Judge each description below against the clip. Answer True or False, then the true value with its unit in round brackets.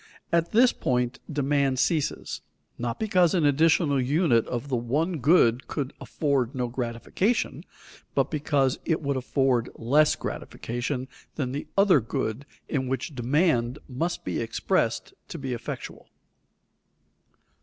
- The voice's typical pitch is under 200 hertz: True (140 Hz)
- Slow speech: True (130 wpm)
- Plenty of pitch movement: False (4.2 semitones)